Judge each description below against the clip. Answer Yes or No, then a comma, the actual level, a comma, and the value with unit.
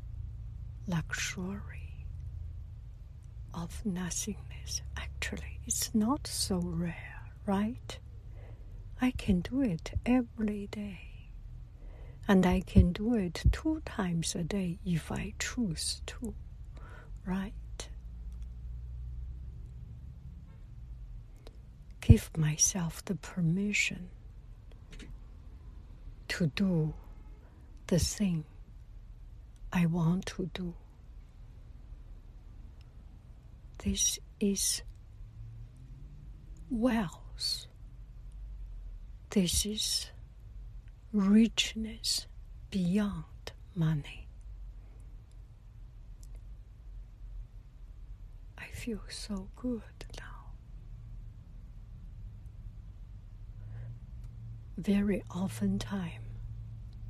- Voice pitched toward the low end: Yes, low, 110 Hz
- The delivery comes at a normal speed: No, slow, 60 wpm